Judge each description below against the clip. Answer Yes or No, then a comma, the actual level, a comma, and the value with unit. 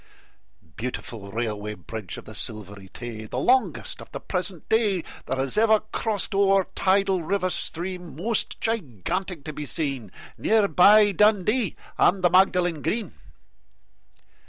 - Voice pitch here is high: No, medium, 180 Hz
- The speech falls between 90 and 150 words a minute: Yes, average, 140 wpm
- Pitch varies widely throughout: Yes, wide, 8.2 semitones